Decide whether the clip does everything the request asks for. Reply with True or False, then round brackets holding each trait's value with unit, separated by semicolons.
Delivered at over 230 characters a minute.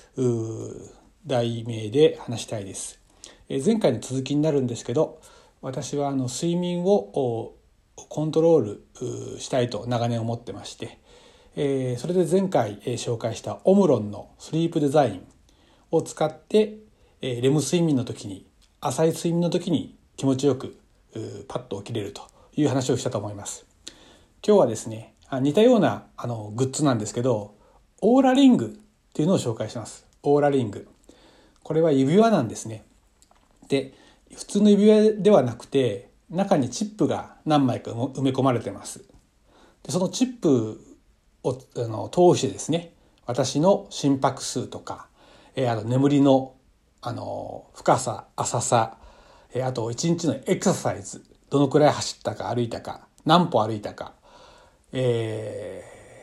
True (280 characters per minute)